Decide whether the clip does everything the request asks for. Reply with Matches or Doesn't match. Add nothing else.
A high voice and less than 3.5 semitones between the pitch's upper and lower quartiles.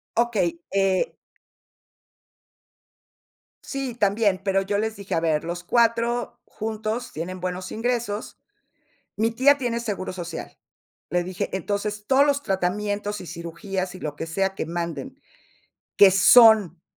Doesn't match